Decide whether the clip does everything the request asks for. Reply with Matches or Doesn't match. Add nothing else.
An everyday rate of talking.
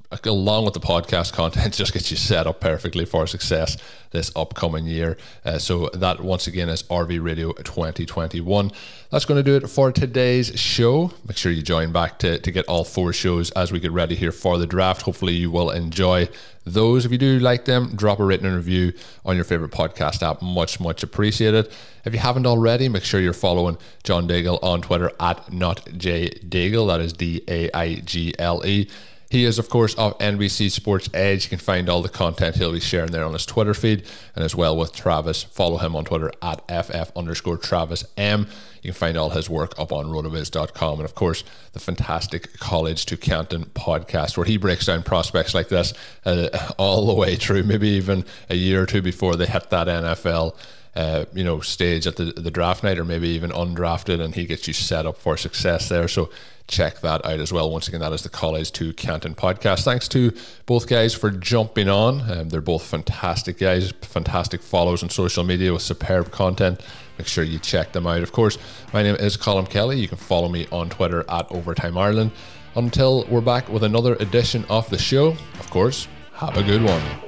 Doesn't match